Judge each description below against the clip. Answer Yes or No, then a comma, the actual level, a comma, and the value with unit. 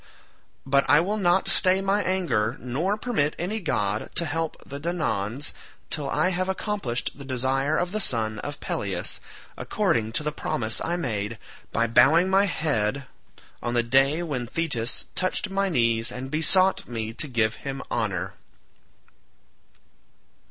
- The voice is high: No, medium, 140 Hz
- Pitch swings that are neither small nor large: No, wide, 7.3 semitones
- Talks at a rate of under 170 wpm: Yes, average, 150 wpm